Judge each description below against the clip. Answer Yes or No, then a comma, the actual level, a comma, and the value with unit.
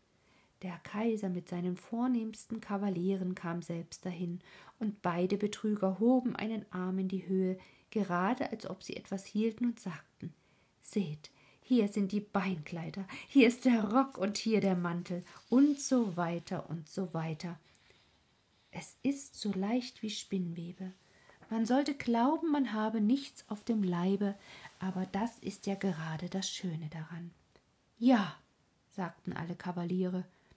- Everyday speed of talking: Yes, average, 140 wpm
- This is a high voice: Yes, high, 195 Hz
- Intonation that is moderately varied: Yes, average, 3.9 semitones